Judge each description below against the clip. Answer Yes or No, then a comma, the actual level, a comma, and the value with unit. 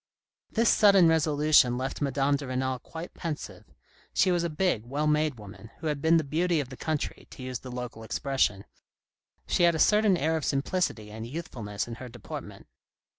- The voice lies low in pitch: No, medium, 145 Hz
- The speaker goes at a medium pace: Yes, average, 185 wpm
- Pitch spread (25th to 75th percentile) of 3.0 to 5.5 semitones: Yes, average, 4.6 semitones